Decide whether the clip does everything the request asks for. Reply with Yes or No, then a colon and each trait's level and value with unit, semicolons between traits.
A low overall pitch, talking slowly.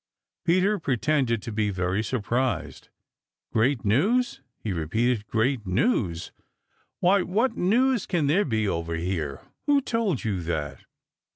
Yes: low, 120 Hz; slow, 130 wpm